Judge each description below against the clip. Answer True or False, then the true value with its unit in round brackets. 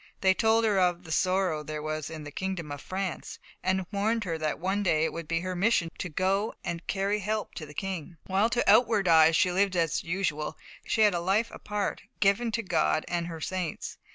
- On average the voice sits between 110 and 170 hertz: False (185 Hz)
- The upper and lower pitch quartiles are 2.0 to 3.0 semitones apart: False (3.5 semitones)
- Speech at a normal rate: False (215 wpm)